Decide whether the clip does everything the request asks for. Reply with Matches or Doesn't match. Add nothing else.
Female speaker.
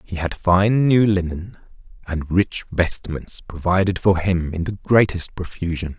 Doesn't match